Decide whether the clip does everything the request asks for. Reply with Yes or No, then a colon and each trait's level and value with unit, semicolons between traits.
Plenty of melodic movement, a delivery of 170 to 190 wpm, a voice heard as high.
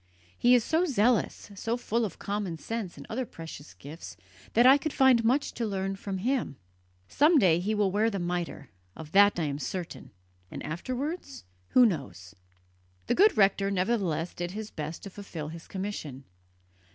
Yes: wide, 6.0 semitones; average, 175 wpm; high, 200 Hz